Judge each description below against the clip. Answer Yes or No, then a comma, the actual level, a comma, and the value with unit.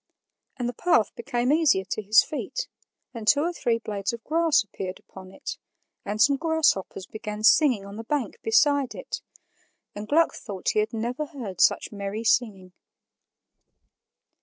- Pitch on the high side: Yes, high, 230 Hz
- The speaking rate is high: No, average, 160 wpm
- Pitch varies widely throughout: Yes, wide, 5.9 semitones